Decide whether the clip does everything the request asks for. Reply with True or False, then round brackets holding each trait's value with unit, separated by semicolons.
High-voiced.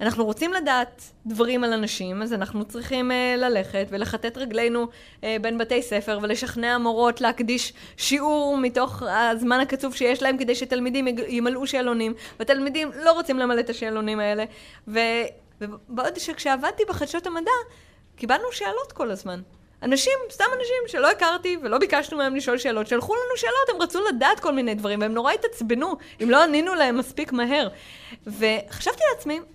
True (250 Hz)